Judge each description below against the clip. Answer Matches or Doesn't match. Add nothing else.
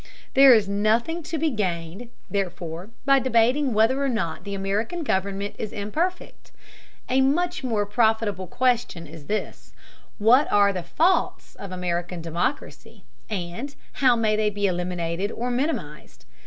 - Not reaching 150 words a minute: Matches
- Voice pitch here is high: Matches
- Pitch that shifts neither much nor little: Doesn't match